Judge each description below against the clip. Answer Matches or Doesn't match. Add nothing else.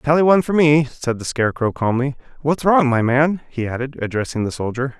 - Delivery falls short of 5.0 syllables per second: Doesn't match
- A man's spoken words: Matches